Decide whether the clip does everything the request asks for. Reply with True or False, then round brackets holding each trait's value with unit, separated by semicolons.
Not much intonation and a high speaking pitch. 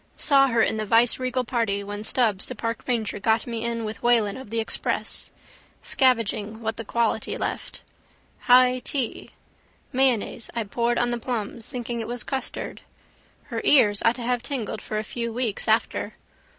True (2.2 semitones; 235 Hz)